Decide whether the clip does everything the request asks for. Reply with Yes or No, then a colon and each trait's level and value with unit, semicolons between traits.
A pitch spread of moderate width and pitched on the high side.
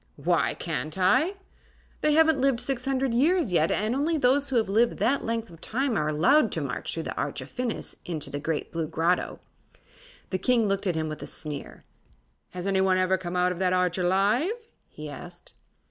No: wide, 7.0 semitones; high, 195 Hz